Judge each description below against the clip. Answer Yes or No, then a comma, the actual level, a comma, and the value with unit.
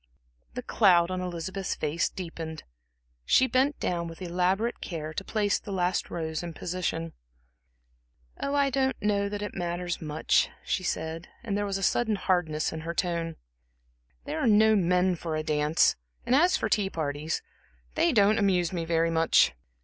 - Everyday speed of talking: Yes, average, 170 wpm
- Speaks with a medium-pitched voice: Yes, medium, 180 Hz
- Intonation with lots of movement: No, average, 3.8 semitones